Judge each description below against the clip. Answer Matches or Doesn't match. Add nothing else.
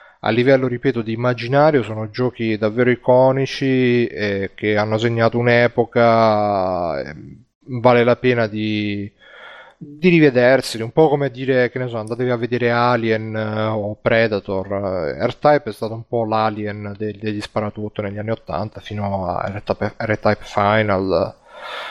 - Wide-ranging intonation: Doesn't match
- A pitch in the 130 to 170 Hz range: Doesn't match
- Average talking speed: Matches